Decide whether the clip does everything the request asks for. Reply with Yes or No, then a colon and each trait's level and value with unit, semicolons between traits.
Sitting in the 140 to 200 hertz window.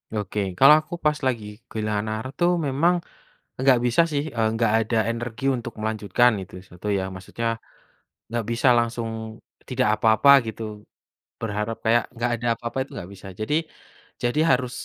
No: low, 115 Hz